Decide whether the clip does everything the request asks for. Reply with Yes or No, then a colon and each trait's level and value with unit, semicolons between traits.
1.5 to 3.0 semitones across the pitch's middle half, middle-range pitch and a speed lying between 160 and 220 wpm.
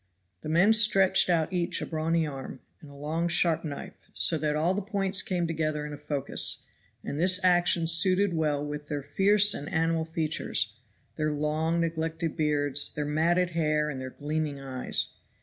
Yes: average, 2.7 semitones; medium, 160 Hz; average, 175 wpm